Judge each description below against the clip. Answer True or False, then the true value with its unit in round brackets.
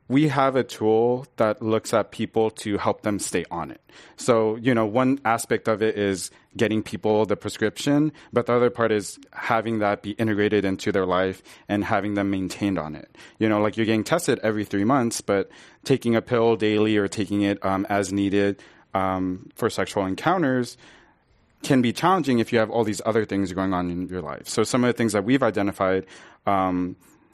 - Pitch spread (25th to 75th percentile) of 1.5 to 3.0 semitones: True (2.6 semitones)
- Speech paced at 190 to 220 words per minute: True (200 wpm)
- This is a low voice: True (110 Hz)